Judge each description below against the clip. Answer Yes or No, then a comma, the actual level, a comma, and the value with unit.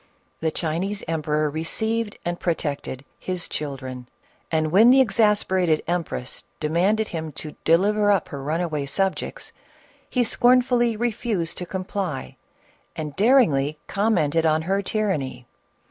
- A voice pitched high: No, medium, 175 Hz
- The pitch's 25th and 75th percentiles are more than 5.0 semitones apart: Yes, wide, 5.5 semitones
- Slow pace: Yes, slow, 130 wpm